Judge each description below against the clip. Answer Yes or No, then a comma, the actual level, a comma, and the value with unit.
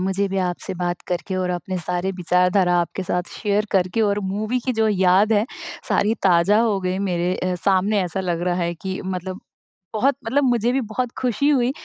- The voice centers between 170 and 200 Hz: Yes, high, 190 Hz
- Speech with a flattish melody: No, average, 3.1 semitones